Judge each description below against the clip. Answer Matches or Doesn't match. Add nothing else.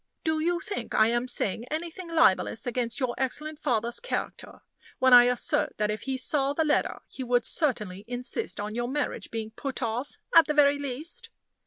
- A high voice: Matches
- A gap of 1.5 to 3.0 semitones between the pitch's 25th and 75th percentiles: Doesn't match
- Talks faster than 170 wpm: Matches